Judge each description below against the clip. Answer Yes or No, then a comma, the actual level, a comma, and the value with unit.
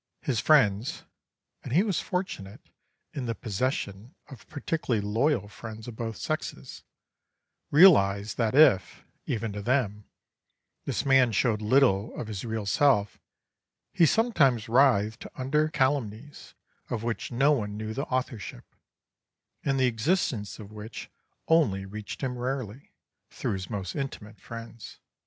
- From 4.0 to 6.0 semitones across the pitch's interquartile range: Yes, average, 4.7 semitones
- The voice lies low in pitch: Yes, low, 115 Hz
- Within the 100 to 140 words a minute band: Yes, slow, 135 wpm